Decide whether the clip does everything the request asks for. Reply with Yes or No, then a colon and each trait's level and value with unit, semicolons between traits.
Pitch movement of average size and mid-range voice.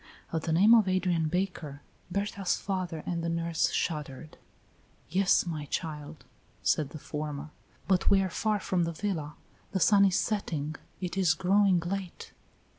Yes: average, 3.7 semitones; medium, 175 Hz